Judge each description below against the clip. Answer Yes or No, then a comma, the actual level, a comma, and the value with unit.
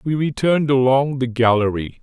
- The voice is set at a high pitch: No, low, 130 Hz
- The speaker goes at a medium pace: Yes, average, 150 wpm